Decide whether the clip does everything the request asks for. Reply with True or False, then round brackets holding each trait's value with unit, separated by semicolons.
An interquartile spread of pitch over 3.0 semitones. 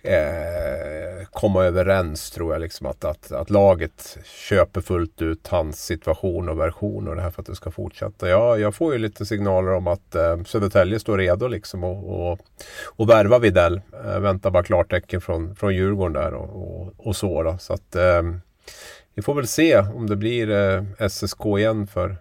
False (2.6 semitones)